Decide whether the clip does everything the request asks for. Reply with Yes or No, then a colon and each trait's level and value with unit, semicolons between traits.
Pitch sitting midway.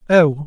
Yes: medium, 155 Hz